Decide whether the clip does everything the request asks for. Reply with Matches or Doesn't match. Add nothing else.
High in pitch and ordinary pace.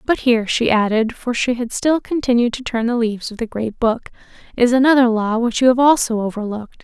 Doesn't match